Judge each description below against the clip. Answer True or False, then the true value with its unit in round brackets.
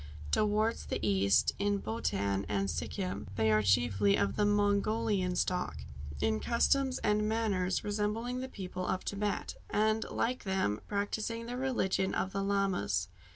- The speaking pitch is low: False (195 Hz)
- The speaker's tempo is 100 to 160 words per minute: True (145 wpm)